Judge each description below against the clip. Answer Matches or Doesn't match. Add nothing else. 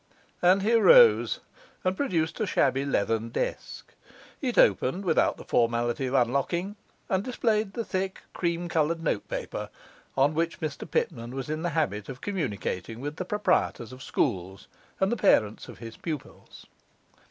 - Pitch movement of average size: Doesn't match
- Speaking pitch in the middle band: Matches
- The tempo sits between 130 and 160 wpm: Matches